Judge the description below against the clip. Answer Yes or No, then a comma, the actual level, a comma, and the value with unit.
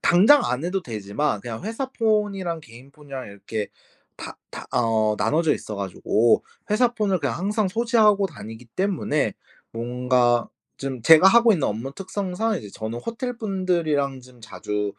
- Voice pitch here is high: No, medium, 150 Hz